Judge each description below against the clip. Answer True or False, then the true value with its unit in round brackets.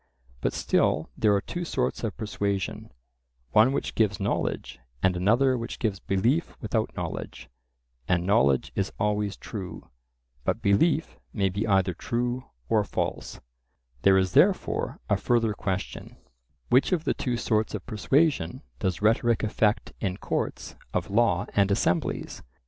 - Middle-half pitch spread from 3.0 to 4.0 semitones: True (3.7 semitones)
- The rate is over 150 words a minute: False (140 wpm)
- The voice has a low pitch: True (105 Hz)